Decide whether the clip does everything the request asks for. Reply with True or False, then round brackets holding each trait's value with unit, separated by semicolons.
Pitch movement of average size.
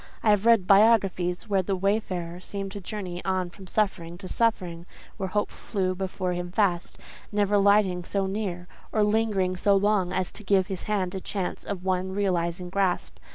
False (2.1 semitones)